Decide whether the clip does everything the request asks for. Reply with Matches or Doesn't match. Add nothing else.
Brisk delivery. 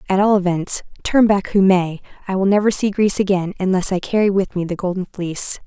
Matches